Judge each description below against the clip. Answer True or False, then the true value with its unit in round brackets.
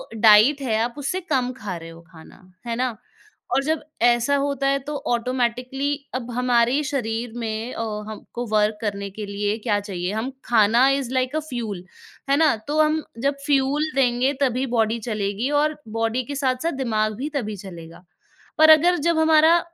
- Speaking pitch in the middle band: False (245 Hz)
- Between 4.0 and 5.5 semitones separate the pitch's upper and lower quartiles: True (4.4 semitones)